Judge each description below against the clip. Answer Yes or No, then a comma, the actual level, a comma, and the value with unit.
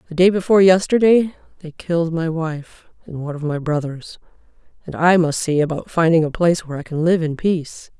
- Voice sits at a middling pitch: Yes, medium, 165 Hz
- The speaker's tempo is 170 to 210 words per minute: Yes, fast, 205 wpm